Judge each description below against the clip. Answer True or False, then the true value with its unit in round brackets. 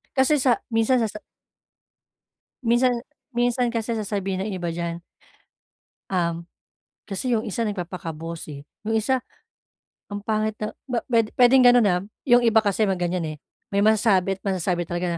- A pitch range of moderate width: True (4.9 semitones)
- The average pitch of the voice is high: True (210 Hz)